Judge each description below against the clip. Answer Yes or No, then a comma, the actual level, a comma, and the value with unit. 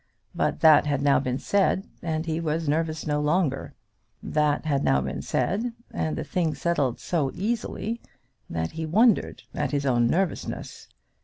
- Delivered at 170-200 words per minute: No, average, 160 wpm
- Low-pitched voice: No, medium, 155 Hz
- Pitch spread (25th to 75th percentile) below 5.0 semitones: Yes, average, 3.8 semitones